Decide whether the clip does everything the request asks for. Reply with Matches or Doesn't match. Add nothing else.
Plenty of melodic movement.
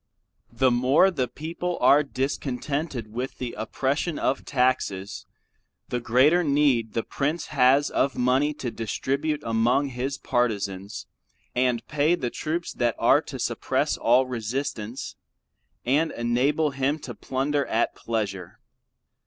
Doesn't match